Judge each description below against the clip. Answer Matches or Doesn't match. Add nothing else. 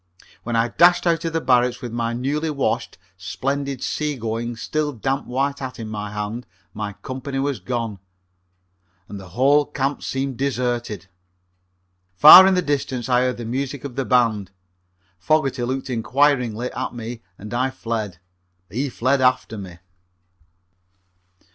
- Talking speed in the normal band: Matches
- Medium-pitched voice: Doesn't match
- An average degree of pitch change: Matches